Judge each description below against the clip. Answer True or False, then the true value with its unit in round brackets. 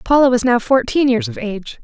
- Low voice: False (250 Hz)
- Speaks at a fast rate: True (230 wpm)